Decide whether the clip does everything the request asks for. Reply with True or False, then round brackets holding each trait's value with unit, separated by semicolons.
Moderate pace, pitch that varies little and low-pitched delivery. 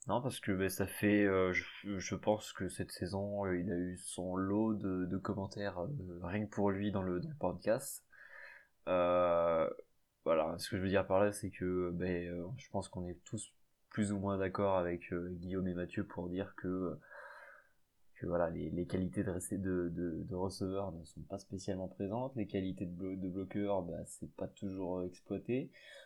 True (205 wpm; 1.9 semitones; 95 Hz)